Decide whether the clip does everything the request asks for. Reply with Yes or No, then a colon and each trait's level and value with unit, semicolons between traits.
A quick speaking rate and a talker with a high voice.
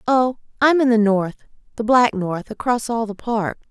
No: average, 180 wpm; high, 225 Hz